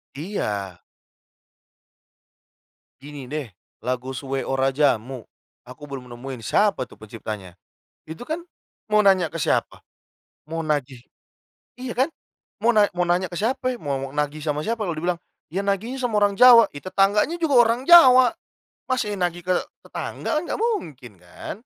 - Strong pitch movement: Yes, wide, 8.8 semitones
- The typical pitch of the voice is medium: Yes, medium, 170 Hz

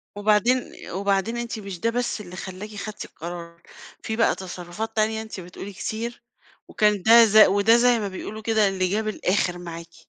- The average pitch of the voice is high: Yes, high, 210 Hz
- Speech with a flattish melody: No, average, 3.0 semitones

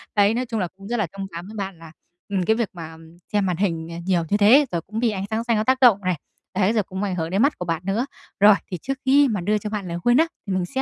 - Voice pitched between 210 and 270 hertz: No, high, 200 Hz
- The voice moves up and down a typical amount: Yes, average, 3.9 semitones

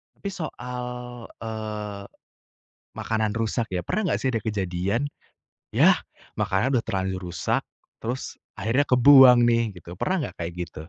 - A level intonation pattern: No, average, 4.4 semitones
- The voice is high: No, low, 110 Hz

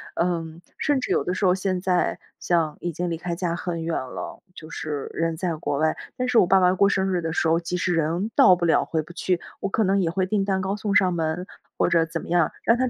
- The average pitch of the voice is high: No, medium, 175 Hz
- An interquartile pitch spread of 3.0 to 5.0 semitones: No, narrow, 2.6 semitones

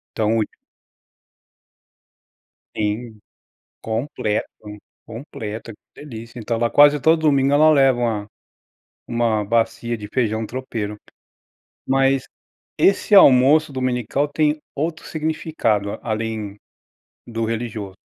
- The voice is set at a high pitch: No, low, 120 Hz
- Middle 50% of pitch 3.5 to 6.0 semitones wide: Yes, average, 4.3 semitones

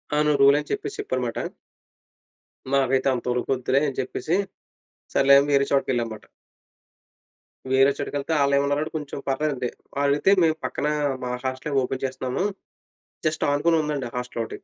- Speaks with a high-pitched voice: No, medium, 140 Hz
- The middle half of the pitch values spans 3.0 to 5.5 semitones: No, narrow, 2.4 semitones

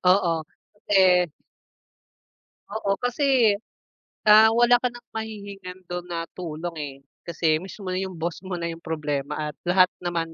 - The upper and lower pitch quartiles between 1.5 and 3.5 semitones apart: No, average, 3.9 semitones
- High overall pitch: No, medium, 180 Hz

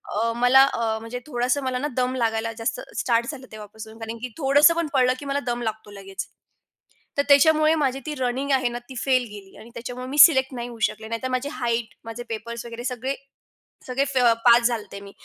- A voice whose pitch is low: No, high, 245 Hz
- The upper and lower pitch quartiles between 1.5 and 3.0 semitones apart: Yes, average, 2.7 semitones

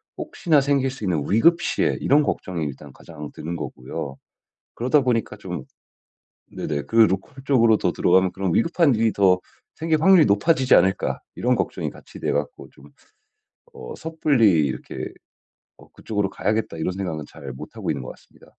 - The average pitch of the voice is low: Yes, low, 110 Hz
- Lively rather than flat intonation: Yes, wide, 7.4 semitones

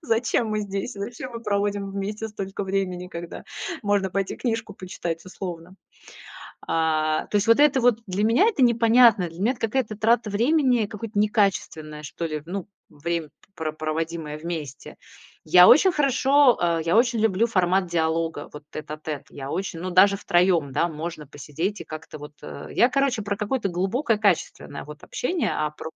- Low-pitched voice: No, high, 195 Hz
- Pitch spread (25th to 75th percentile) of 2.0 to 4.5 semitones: No, wide, 5.5 semitones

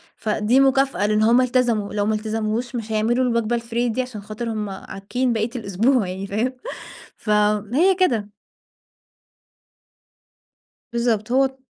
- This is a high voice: Yes, high, 230 Hz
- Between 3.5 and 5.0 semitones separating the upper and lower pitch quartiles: No, average, 2.9 semitones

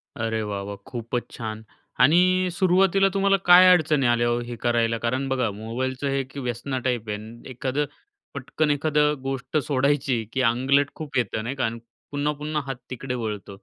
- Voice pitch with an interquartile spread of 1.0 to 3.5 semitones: No, average, 3.9 semitones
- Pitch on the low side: Yes, low, 130 Hz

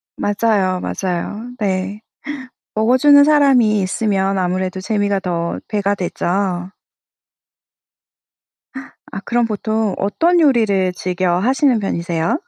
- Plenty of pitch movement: No, average, 3.5 semitones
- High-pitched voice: Yes, high, 200 Hz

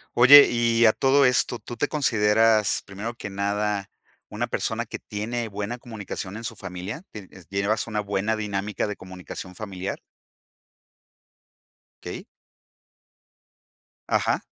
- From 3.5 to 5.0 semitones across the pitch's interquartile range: No, average, 2.8 semitones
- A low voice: Yes, low, 105 Hz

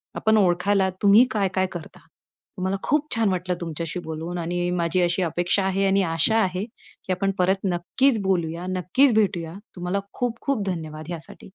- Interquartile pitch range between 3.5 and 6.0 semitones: No, narrow, 2.5 semitones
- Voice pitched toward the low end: No, medium, 185 Hz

